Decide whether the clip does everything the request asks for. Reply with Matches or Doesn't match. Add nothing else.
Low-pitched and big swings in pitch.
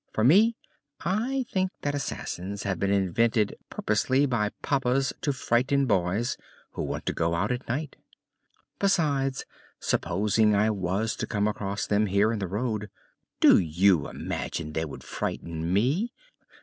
Matches